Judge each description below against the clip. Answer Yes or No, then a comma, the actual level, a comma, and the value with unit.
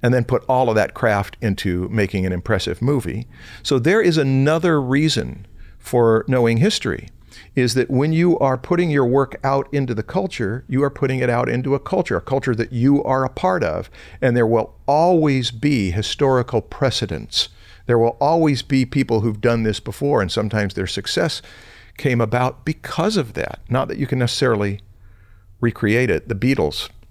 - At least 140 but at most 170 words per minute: No, average, 180 wpm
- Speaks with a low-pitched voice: Yes, low, 125 Hz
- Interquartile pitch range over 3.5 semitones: Yes, average, 4.0 semitones